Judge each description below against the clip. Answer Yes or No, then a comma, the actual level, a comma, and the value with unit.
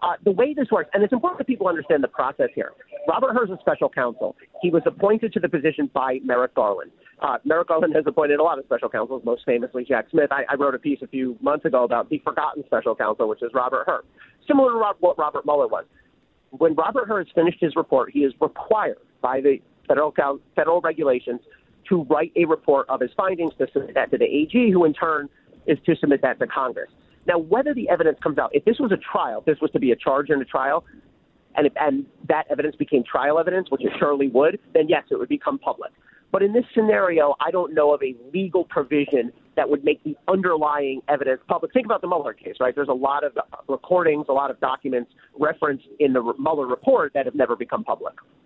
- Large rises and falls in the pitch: Yes, wide, 7.4 semitones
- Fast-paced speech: Yes, fast, 230 wpm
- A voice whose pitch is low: No, medium, 160 Hz